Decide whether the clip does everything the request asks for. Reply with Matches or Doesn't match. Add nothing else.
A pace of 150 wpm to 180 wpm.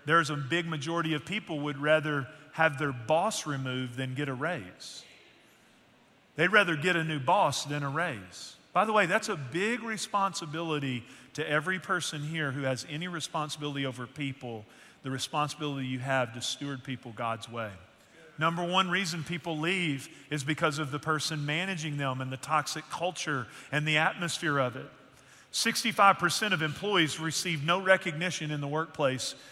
Matches